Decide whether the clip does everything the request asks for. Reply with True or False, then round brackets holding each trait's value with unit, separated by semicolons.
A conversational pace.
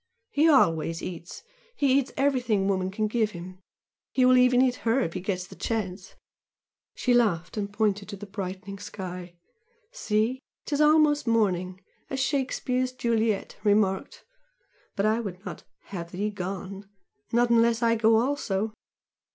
True (150 wpm)